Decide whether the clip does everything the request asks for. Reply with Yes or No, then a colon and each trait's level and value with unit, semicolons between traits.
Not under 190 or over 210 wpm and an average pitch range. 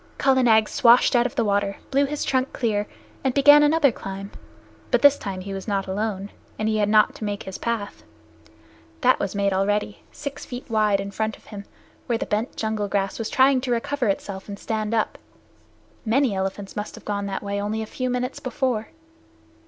Yes: average, 200 wpm; average, 3.8 semitones